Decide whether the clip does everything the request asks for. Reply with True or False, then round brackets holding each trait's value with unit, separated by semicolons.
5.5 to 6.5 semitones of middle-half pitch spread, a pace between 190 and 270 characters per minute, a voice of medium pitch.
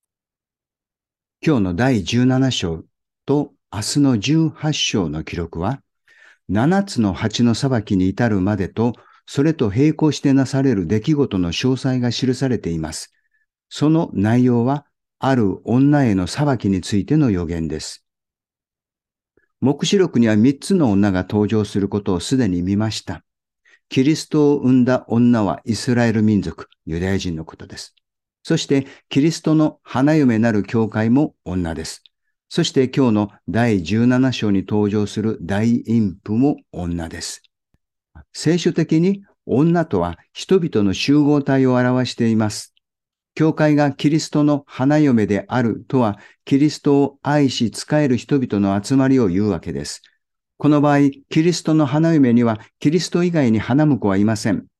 False (6.1 semitones; 265 characters per minute; 125 Hz)